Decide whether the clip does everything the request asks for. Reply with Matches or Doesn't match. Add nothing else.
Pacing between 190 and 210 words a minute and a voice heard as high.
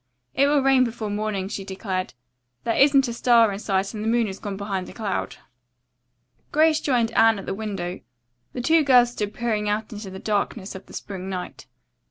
Matches